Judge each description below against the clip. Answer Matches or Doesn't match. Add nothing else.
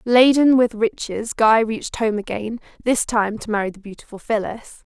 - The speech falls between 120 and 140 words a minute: Doesn't match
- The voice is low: Doesn't match